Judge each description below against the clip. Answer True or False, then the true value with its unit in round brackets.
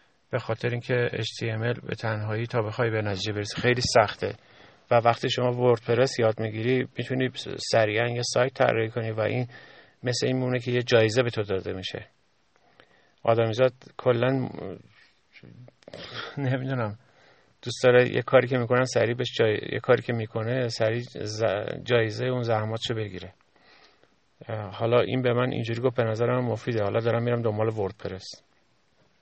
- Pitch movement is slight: True (2.1 semitones)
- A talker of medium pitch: False (120 Hz)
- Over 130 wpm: True (150 wpm)